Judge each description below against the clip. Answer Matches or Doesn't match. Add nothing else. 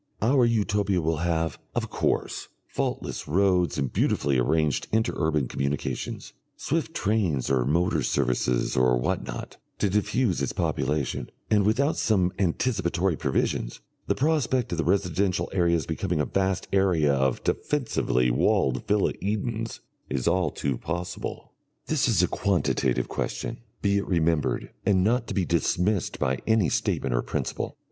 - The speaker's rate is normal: Matches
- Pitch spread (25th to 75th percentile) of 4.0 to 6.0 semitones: Matches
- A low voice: Matches